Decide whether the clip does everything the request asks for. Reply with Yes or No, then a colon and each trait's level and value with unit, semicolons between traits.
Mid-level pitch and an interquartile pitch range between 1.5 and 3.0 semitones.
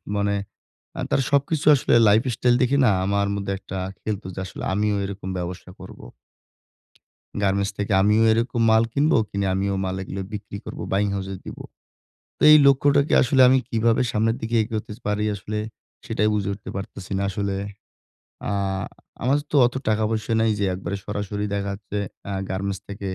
No: low, 105 Hz; narrow, 2.5 semitones